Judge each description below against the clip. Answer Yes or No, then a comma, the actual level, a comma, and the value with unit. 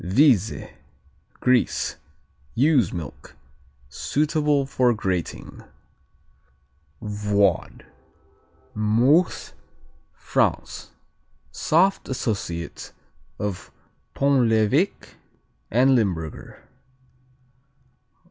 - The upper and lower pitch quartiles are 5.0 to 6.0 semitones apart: Yes, wide, 5.5 semitones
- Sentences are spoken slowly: Yes, slow, 55 wpm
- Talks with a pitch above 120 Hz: No, low, 115 Hz